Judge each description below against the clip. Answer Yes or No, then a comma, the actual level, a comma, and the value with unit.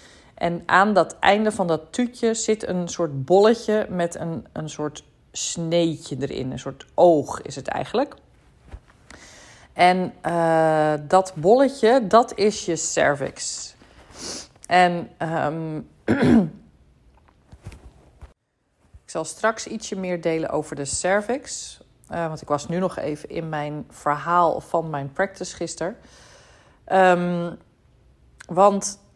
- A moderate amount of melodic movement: Yes, average, 3.9 semitones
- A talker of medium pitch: Yes, medium, 170 Hz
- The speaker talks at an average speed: No, slow, 120 wpm